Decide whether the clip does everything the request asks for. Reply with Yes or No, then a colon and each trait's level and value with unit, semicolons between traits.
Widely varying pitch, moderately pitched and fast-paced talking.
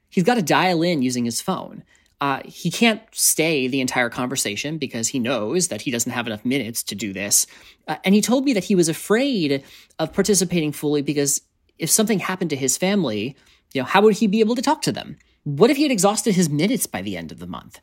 Yes: wide, 7.5 semitones; medium, 165 Hz; fast, 235 wpm